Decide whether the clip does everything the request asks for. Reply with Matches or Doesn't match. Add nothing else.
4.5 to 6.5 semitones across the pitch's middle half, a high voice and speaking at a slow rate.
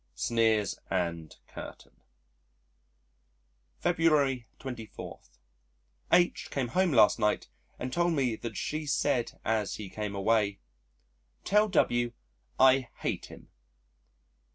Doesn't match